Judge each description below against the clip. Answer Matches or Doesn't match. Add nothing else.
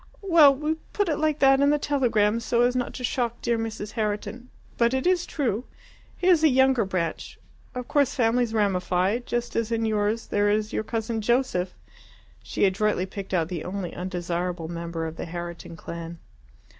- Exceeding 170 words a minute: Matches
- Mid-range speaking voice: Doesn't match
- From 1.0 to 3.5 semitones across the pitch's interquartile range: Doesn't match